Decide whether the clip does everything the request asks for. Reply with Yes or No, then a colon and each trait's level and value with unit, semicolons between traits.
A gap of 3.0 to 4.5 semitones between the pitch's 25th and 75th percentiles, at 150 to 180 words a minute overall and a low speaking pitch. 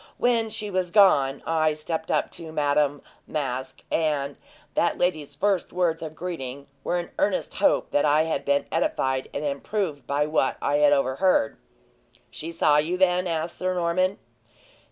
No: average, 4.1 semitones; average, 160 wpm; medium, 155 Hz